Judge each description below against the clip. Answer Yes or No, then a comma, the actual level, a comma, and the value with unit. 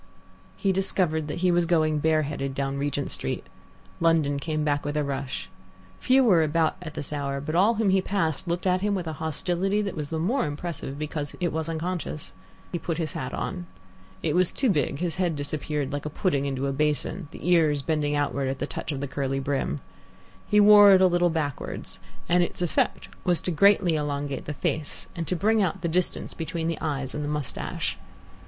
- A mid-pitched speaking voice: Yes, medium, 160 Hz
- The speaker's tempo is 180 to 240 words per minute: Yes, fast, 205 wpm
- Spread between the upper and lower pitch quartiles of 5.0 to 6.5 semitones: No, average, 3.6 semitones